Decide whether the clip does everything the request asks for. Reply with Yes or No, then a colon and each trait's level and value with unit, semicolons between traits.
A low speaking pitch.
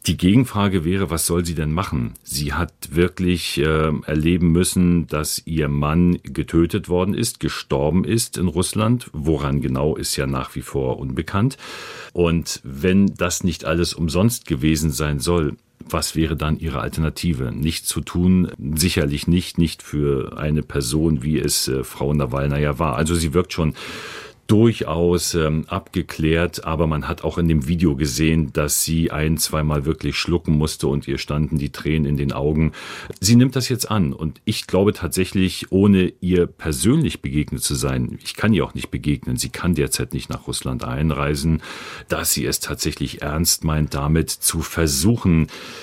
Yes: very low, 80 Hz